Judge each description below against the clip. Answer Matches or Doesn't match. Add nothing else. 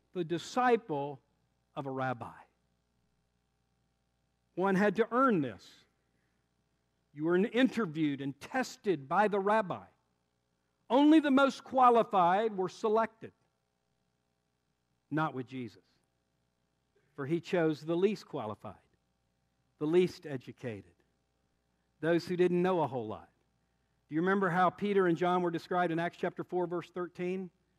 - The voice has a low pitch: Doesn't match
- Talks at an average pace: Doesn't match